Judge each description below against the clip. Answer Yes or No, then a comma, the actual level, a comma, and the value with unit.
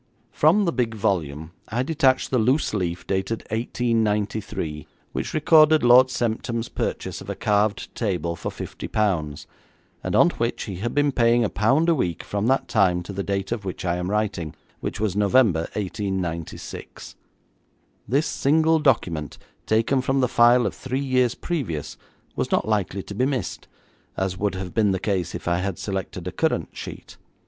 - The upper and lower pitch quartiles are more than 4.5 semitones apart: Yes, average, 5.3 semitones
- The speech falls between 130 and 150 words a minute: No, average, 175 wpm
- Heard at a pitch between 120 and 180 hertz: No, low, 105 Hz